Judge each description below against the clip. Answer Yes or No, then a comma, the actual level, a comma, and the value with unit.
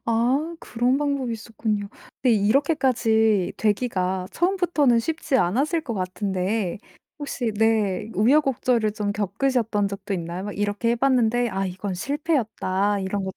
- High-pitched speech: Yes, high, 220 Hz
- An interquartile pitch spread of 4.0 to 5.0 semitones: Yes, average, 4.4 semitones